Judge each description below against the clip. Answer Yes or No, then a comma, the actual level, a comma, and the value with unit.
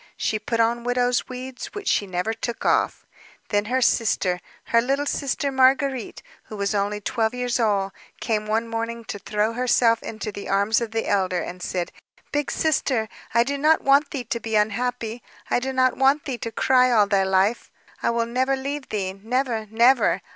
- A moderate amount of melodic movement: Yes, average, 3.4 semitones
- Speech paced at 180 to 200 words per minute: Yes, average, 190 wpm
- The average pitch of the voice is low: No, high, 230 Hz